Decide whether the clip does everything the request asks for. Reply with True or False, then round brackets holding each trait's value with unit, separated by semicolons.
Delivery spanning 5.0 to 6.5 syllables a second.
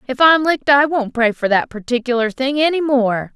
True (5.3 syllables/s)